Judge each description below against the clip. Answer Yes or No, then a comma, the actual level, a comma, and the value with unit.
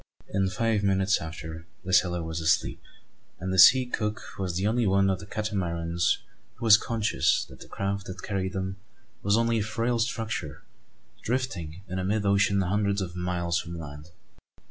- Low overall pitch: Yes, very low, 95 Hz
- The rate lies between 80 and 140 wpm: No, average, 170 wpm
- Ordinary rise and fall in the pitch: Yes, average, 3.4 semitones